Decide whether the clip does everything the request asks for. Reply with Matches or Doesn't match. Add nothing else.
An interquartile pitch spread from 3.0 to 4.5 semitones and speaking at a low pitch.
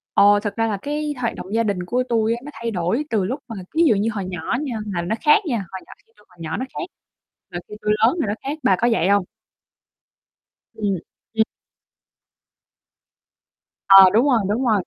Doesn't match